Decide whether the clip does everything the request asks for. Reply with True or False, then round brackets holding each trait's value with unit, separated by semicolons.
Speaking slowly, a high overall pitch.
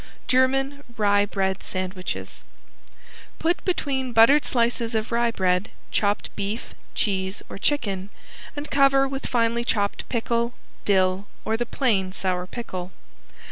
True (125 wpm; 225 Hz)